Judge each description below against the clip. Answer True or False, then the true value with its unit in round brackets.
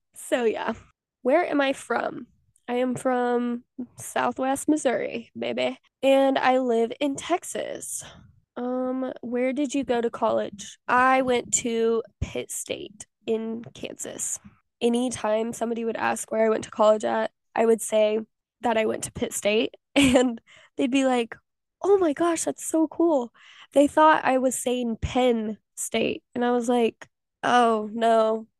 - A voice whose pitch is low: False (245 Hz)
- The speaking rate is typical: True (155 wpm)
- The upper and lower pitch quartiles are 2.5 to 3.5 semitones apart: True (3.0 semitones)